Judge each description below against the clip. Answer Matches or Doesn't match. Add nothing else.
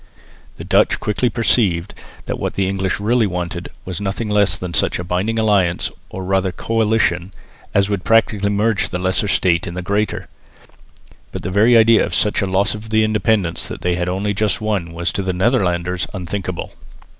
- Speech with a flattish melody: Doesn't match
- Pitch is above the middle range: Doesn't match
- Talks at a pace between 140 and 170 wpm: Doesn't match